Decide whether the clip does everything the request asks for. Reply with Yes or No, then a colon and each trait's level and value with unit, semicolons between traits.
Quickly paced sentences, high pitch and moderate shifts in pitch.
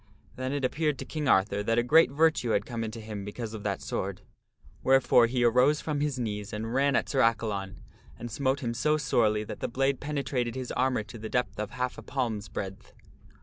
No: fast, 215 wpm; low, 120 Hz; average, 3.8 semitones